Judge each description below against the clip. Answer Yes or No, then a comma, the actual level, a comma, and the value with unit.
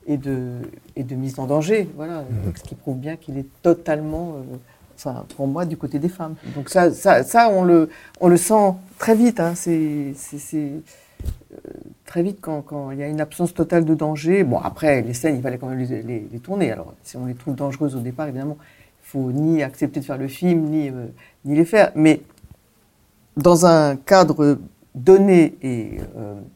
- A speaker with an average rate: Yes, average, 210 wpm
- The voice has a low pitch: No, medium, 150 Hz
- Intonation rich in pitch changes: No, average, 3.9 semitones